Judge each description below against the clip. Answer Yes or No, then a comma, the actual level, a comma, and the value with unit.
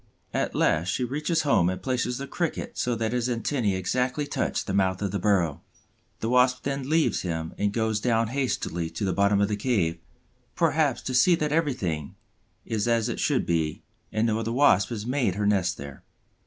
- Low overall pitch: Yes, low, 115 Hz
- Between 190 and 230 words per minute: Yes, average, 195 wpm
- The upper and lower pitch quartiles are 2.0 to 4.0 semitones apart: No, average, 5.2 semitones